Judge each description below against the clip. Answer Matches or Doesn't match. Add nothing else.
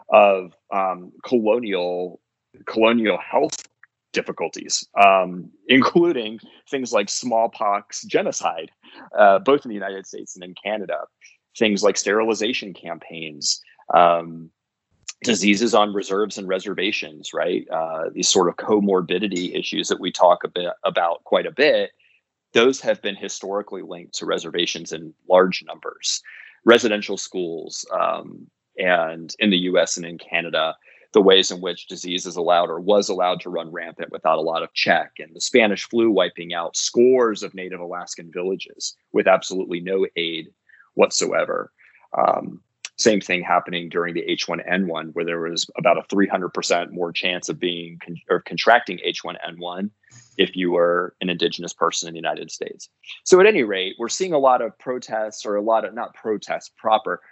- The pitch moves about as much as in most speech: Matches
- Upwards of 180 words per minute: Doesn't match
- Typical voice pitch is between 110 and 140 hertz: Doesn't match